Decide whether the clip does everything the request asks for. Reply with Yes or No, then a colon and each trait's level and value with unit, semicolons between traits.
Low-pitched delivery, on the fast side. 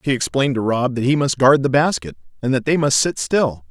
Yes: low, 130 Hz; fast, 260 wpm